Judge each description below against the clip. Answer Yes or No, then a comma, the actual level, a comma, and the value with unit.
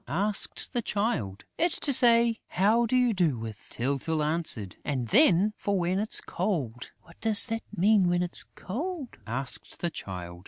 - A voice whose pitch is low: No, medium, 185 Hz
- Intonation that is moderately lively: No, wide, 8.7 semitones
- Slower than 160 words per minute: No, average, 165 wpm